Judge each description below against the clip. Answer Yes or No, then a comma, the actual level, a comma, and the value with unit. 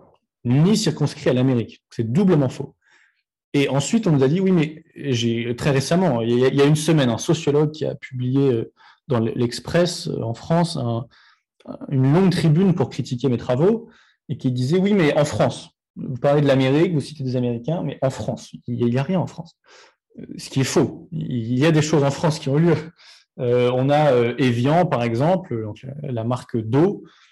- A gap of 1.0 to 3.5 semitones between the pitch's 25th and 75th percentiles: No, average, 4.4 semitones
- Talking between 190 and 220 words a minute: Yes, average, 200 wpm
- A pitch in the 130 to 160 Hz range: Yes, medium, 140 Hz